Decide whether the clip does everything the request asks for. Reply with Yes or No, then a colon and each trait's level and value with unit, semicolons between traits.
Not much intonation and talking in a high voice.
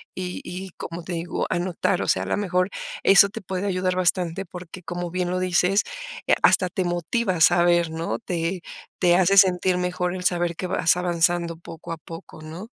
No: narrow, 1.2 semitones; medium, 180 Hz